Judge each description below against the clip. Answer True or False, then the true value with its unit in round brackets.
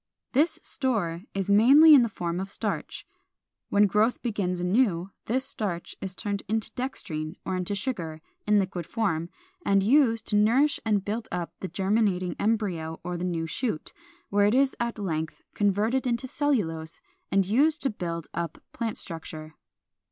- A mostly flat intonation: False (4.8 semitones)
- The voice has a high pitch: True (200 Hz)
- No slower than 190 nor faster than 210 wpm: False (160 wpm)